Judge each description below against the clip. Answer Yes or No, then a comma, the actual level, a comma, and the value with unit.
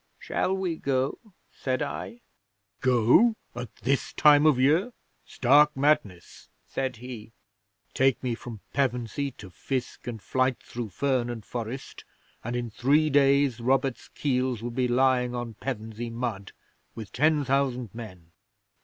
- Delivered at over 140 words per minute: No, slow, 135 wpm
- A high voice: No, low, 130 Hz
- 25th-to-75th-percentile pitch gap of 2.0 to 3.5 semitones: Yes, average, 2.8 semitones